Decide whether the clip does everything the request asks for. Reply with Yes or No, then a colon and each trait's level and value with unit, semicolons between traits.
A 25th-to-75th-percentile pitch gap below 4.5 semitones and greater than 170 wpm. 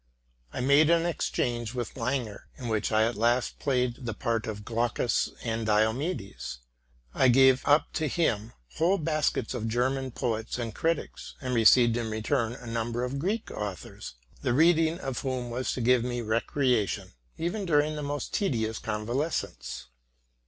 No: average, 4.0 semitones; average, 160 wpm